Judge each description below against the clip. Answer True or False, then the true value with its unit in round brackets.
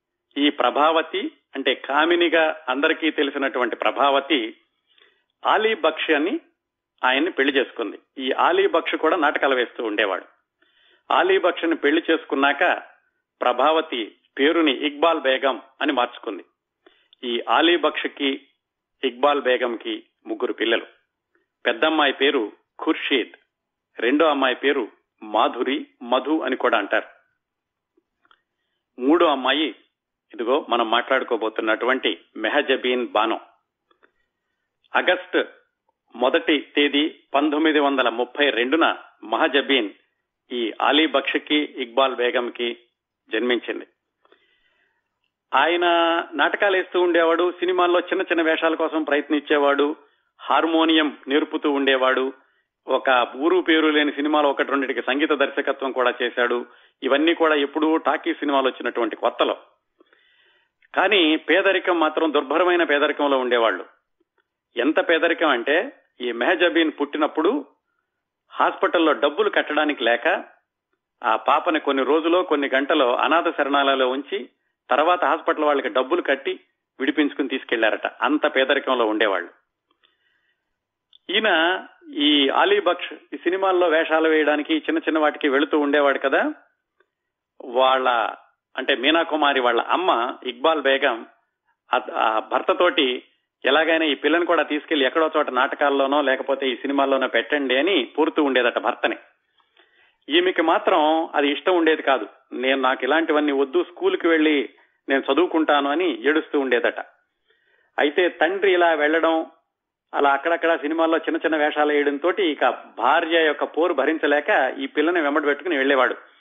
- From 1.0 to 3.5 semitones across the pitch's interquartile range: False (4.2 semitones)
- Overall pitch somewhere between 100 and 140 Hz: False (155 Hz)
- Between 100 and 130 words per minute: True (110 wpm)